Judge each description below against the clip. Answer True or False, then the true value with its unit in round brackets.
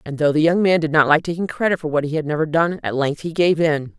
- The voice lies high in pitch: False (160 Hz)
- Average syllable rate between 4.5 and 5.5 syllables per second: False (6.2 syllables/s)